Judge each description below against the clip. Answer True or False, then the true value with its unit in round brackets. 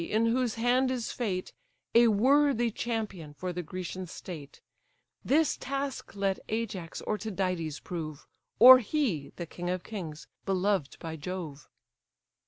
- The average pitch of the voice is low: False (195 Hz)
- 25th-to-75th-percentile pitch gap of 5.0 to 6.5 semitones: True (5.4 semitones)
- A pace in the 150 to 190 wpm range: False (135 wpm)